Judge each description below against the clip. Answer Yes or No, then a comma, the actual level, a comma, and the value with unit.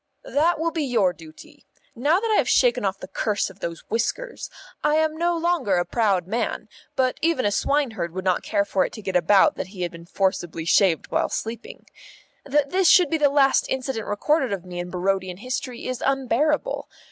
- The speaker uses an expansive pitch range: Yes, wide, 8.1 semitones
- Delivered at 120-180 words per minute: No, fast, 205 wpm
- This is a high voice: Yes, high, 230 Hz